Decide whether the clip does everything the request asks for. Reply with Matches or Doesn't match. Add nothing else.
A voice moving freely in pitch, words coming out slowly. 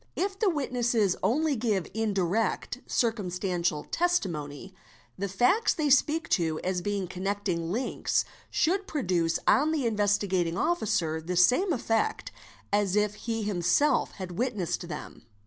Matches